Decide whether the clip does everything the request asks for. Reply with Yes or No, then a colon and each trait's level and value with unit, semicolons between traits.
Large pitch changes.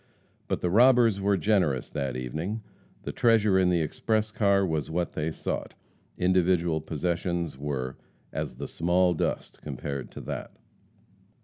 No: average, 4.4 semitones